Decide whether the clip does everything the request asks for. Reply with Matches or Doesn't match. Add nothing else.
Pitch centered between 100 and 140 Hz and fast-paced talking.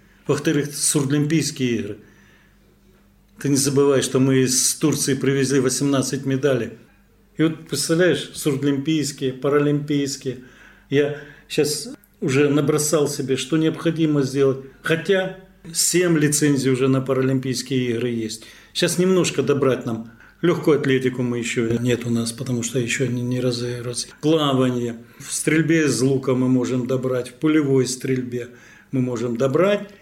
Doesn't match